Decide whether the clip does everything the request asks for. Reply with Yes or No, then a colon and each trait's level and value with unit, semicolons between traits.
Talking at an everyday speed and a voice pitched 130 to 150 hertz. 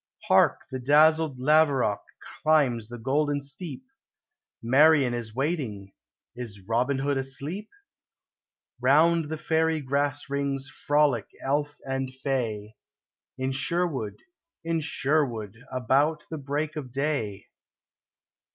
No: slow, 105 wpm; medium, 140 Hz